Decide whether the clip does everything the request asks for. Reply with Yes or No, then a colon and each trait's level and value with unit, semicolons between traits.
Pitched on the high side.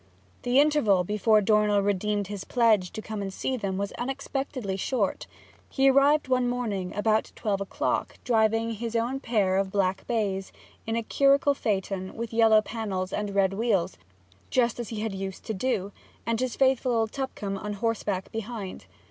Yes: high, 220 Hz